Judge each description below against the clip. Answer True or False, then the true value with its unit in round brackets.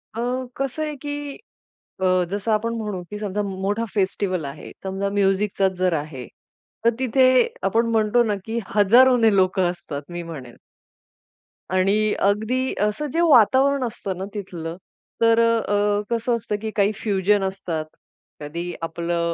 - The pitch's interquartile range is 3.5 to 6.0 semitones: True (3.8 semitones)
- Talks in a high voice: True (205 Hz)